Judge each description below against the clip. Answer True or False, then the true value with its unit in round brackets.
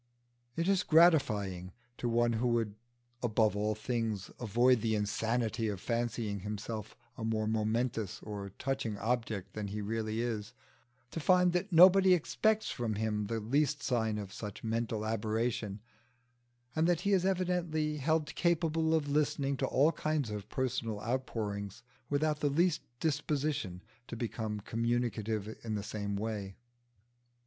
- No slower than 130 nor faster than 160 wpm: True (145 wpm)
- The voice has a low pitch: True (115 Hz)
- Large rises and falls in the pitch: True (5.9 semitones)